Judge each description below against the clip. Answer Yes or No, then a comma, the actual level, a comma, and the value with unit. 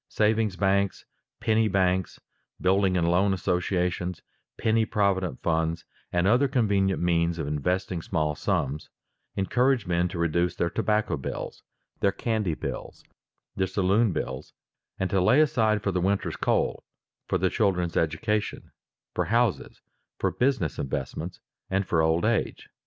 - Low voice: Yes, very low, 95 Hz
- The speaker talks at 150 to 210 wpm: No, average, 140 wpm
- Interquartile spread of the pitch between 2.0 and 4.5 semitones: Yes, average, 3.5 semitones